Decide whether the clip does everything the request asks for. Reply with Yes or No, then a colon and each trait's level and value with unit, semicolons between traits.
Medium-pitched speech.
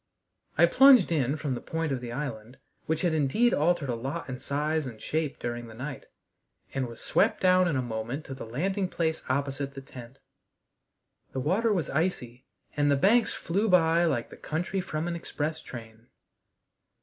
Yes: medium, 145 Hz